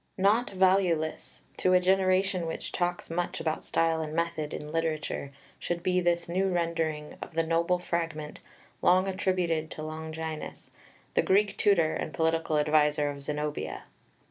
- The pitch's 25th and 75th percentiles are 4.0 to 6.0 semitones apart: No, narrow, 2.6 semitones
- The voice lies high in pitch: No, medium, 165 Hz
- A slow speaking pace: No, average, 145 wpm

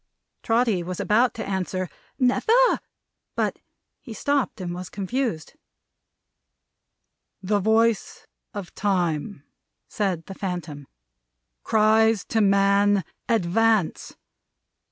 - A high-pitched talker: Yes, high, 200 Hz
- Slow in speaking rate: Yes, slow, 95 wpm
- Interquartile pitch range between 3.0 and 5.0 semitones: Yes, average, 3.6 semitones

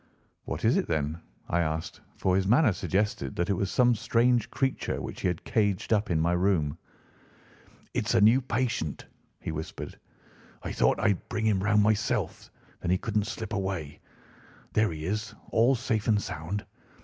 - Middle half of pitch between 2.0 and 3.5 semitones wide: No, average, 4.2 semitones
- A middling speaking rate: Yes, average, 175 wpm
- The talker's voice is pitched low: Yes, low, 100 Hz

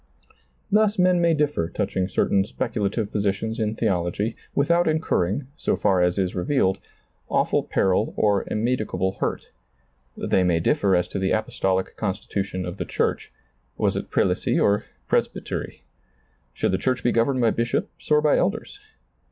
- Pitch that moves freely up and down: Yes, wide, 6.3 semitones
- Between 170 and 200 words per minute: No, average, 160 wpm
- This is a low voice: Yes, low, 105 Hz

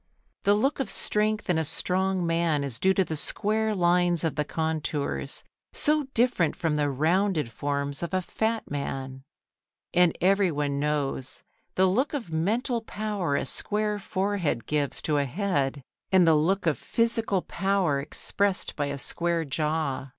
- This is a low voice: No, medium, 170 Hz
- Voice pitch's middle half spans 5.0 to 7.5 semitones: Yes, wide, 5.4 semitones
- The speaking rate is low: No, average, 160 wpm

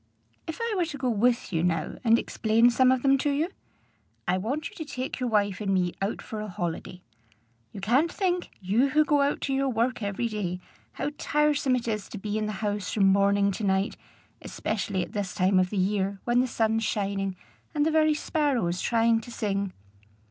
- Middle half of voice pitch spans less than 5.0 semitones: No, average, 5.3 semitones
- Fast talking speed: Yes, fast, 210 wpm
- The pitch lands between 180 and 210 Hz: No, high, 220 Hz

